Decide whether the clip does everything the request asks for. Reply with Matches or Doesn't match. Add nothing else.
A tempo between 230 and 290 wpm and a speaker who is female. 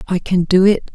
Matches